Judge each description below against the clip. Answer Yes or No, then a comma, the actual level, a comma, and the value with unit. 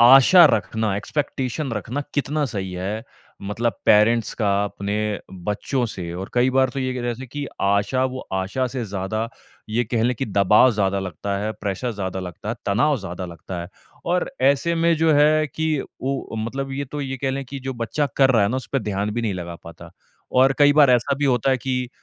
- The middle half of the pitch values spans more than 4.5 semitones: Yes, average, 5.1 semitones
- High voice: No, low, 120 Hz